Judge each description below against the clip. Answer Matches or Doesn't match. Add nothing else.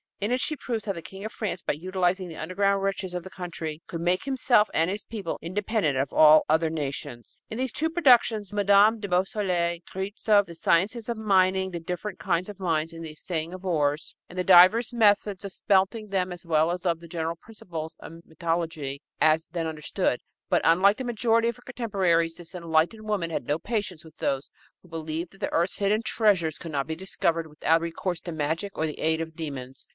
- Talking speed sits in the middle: Doesn't match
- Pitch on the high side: Doesn't match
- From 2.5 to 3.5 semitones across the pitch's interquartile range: Doesn't match